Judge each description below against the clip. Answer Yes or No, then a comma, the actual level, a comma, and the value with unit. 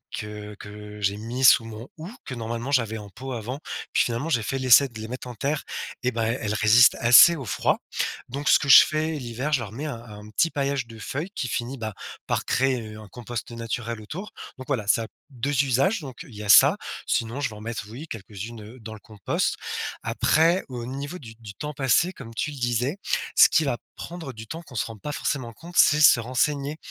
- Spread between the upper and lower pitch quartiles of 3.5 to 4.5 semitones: Yes, average, 4.1 semitones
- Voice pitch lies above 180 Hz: No, low, 120 Hz